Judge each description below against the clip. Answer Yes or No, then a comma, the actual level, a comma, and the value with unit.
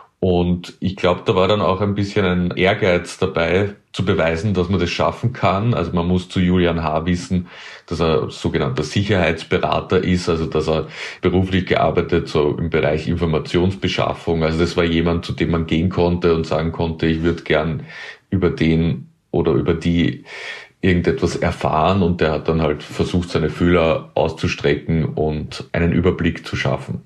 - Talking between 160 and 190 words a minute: Yes, average, 170 wpm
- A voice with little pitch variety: Yes, narrow, 2.0 semitones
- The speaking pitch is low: Yes, very low, 85 Hz